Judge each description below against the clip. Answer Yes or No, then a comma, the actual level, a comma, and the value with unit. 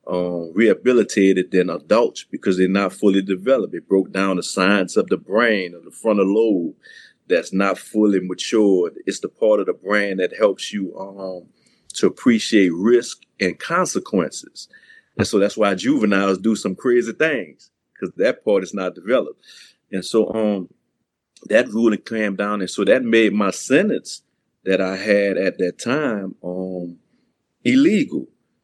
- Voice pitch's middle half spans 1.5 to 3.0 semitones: Yes, average, 2.7 semitones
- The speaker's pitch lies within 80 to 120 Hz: Yes, low, 100 Hz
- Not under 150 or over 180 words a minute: Yes, average, 160 wpm